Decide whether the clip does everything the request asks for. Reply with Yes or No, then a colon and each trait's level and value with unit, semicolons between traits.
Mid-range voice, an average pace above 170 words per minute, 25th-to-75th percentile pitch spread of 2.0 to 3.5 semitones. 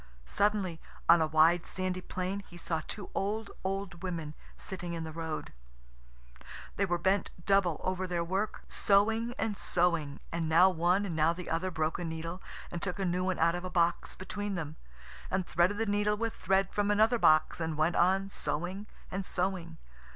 Yes: medium, 180 Hz; average, 185 wpm; average, 2.8 semitones